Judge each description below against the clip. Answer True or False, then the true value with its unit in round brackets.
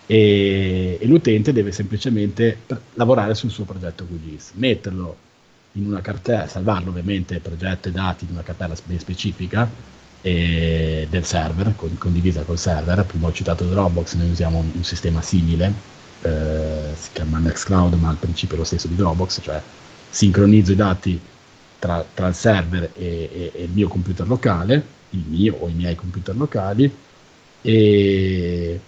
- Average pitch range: True (3.4 semitones)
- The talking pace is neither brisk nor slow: True (160 wpm)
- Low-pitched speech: True (90 Hz)